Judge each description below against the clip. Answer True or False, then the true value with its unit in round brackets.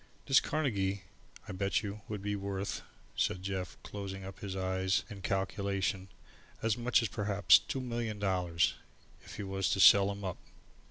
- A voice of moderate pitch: False (100 Hz)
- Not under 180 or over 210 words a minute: False (165 wpm)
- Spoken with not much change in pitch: True (1.3 semitones)